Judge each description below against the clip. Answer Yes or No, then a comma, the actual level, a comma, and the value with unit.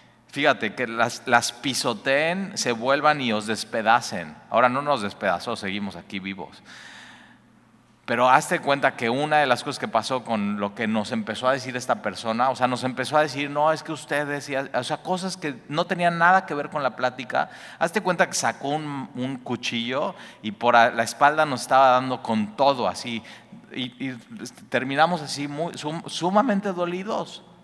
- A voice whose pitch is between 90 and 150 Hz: Yes, low, 135 Hz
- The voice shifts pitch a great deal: No, average, 4.6 semitones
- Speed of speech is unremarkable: Yes, average, 180 wpm